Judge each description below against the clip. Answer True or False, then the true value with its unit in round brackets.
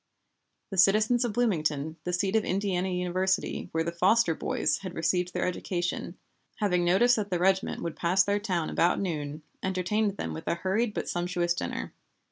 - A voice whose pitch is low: False (180 Hz)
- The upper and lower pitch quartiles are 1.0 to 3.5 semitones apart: True (2.5 semitones)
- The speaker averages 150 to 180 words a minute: True (175 wpm)